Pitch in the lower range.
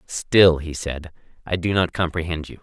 Yes: very low, 85 Hz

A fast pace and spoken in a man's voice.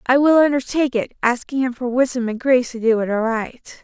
No: fast, 220 wpm; female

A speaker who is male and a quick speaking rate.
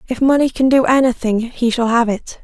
No: female; fast, 220 wpm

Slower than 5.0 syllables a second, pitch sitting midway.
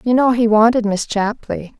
No: 4.8 syllables/s; high, 225 Hz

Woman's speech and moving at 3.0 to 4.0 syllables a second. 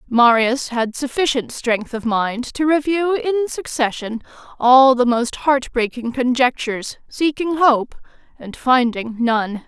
Yes: female; 3.9 syllables/s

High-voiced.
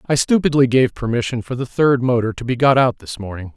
No: low, 125 Hz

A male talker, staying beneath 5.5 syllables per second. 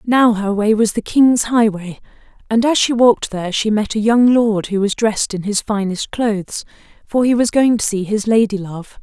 No: female; 5.0 syllables/s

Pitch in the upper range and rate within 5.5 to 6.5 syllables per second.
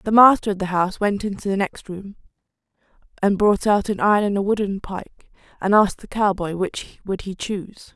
Yes: high, 200 Hz; 5.6 syllables/s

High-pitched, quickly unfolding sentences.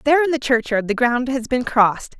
Yes: very high, 250 Hz; fast, 245 wpm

